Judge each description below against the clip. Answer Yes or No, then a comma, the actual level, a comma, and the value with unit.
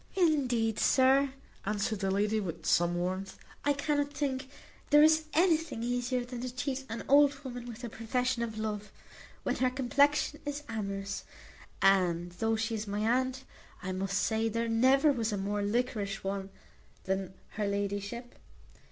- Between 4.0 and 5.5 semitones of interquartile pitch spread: Yes, average, 4.7 semitones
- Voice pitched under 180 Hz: No, high, 230 Hz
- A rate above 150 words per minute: Yes, average, 160 wpm